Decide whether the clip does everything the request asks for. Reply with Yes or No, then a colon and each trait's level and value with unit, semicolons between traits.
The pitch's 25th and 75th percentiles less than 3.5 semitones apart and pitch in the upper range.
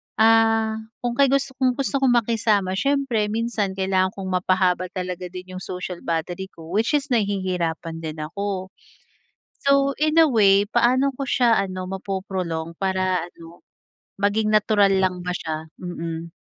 No: average, 3.9 semitones; high, 195 Hz